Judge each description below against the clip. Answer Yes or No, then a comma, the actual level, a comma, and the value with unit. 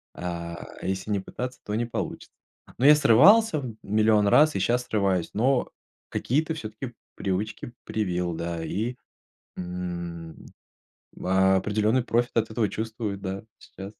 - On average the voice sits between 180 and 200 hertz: No, low, 105 Hz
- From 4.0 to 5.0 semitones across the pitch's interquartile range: Yes, average, 4.5 semitones